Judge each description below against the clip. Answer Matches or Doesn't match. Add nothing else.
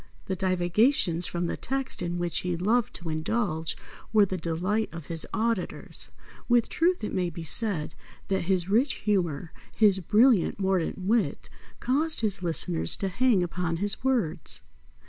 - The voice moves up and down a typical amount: Matches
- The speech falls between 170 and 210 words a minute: Doesn't match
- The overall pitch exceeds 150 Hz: Matches